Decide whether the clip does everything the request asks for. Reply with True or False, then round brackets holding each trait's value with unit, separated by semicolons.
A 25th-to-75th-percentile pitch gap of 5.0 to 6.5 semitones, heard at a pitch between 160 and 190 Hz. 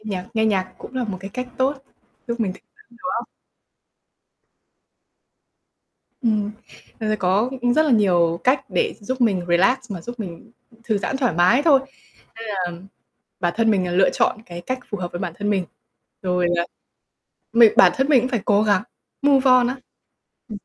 False (5.3 semitones; 215 Hz)